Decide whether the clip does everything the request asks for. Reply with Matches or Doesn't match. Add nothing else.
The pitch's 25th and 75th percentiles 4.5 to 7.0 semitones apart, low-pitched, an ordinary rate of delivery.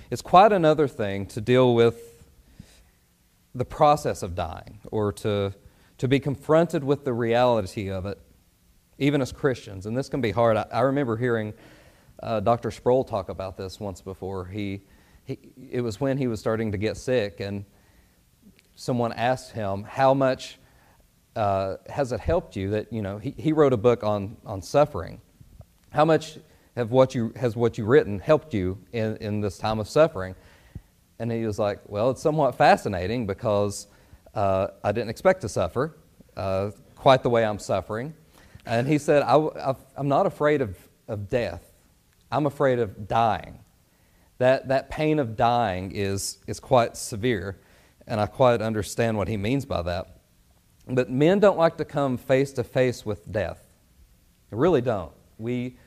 Matches